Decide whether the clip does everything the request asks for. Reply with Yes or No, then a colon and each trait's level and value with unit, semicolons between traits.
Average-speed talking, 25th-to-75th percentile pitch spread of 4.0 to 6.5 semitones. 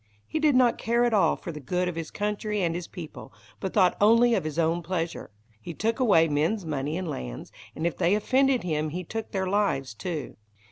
No: fast, 220 wpm; average, 5.1 semitones